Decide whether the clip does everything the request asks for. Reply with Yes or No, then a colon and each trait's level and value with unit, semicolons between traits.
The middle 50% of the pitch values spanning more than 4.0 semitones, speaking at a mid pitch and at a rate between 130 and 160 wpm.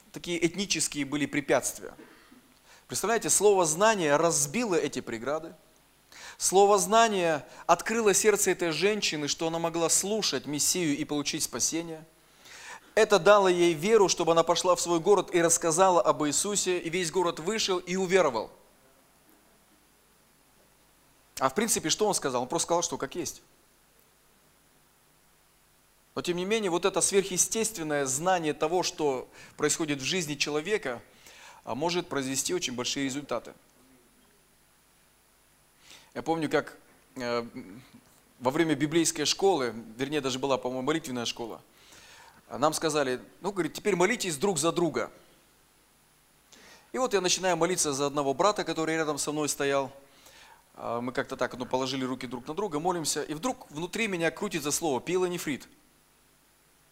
Yes: average, 4.5 semitones; medium, 165 Hz; average, 135 wpm